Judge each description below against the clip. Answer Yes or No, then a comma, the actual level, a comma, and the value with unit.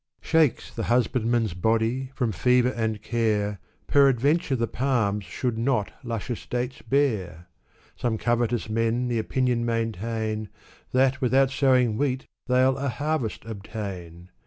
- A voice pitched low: Yes, low, 120 Hz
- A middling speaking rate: No, slow, 125 wpm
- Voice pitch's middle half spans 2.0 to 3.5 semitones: Yes, average, 2.9 semitones